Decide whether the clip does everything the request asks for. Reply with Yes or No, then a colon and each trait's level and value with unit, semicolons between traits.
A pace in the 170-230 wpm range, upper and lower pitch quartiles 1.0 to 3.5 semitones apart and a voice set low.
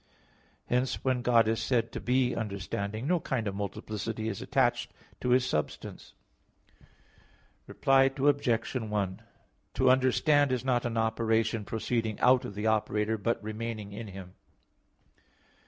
No: slow, 135 wpm; average, 3.0 semitones; low, 115 Hz